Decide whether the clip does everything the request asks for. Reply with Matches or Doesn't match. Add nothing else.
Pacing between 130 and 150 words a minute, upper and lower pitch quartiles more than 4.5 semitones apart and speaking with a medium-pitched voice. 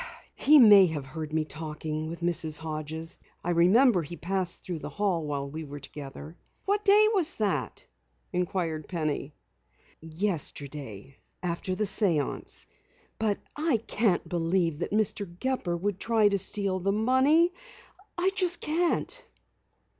Matches